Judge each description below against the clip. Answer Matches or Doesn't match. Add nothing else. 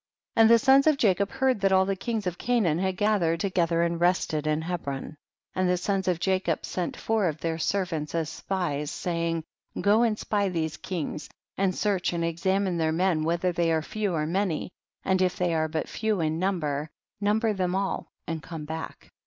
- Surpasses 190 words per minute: Matches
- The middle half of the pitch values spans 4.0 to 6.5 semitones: Doesn't match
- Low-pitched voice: Doesn't match